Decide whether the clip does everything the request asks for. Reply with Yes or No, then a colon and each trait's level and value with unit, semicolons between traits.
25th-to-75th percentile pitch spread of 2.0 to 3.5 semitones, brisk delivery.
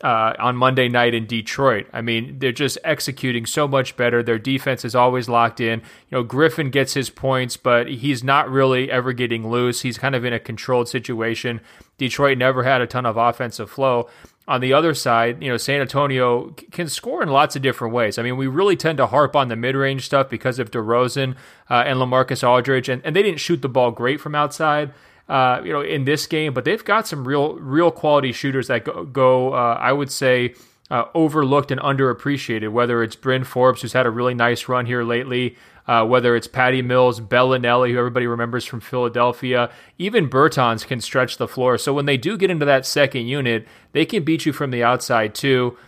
Yes: narrow, 2.5 semitones; fast, 210 wpm